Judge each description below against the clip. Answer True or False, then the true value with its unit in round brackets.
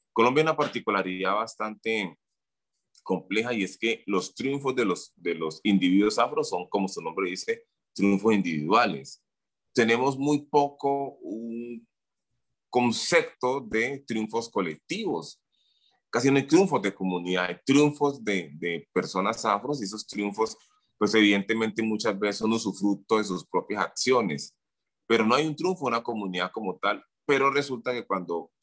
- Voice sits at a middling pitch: False (115 Hz)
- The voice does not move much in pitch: False (5.4 semitones)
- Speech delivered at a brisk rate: False (150 wpm)